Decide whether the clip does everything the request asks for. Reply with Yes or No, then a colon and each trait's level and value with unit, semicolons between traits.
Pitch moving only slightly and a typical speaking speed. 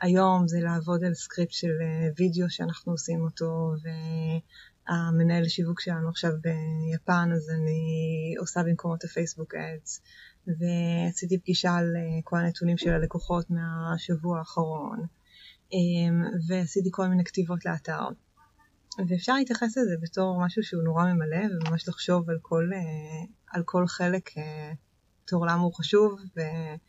Yes: narrow, 1.5 semitones; average, 125 wpm